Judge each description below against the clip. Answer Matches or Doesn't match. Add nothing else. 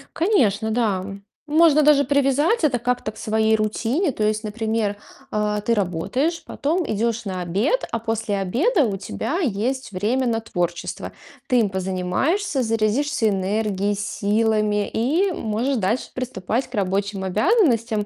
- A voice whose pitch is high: Matches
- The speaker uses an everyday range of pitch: Matches